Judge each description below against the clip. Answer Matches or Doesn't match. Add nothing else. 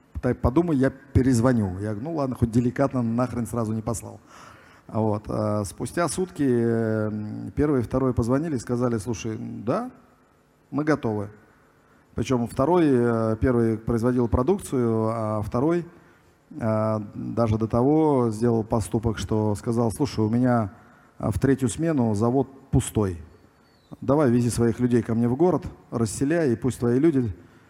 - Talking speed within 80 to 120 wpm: Doesn't match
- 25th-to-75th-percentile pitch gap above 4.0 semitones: Doesn't match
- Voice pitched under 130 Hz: Matches